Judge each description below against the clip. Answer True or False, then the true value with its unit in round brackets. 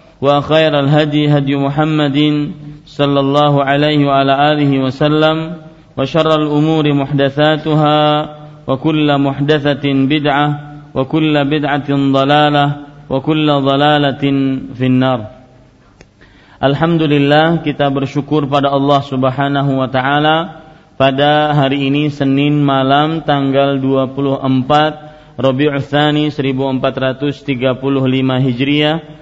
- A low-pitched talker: False (145 Hz)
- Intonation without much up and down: True (1.7 semitones)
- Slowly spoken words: True (75 wpm)